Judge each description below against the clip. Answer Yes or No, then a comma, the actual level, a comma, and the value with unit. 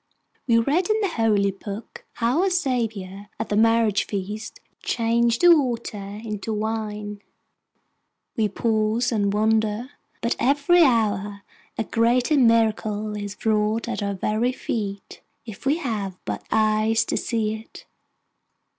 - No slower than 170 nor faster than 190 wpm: No, slow, 135 wpm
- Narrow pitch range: Yes, narrow, 2.2 semitones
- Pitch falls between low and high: No, high, 220 Hz